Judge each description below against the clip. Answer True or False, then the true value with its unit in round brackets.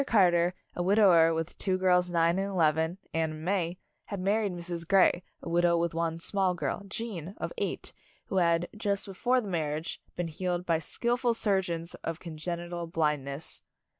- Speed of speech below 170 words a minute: False (175 wpm)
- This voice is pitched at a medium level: True (175 Hz)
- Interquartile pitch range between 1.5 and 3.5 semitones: True (2.6 semitones)